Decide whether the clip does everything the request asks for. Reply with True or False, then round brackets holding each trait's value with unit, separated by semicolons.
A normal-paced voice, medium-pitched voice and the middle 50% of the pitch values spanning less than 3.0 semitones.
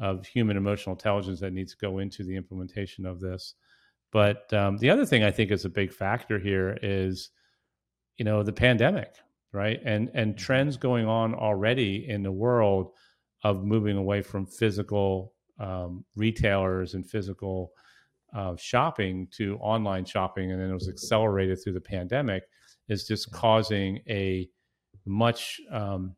False (155 wpm; 100 Hz; 2.6 semitones)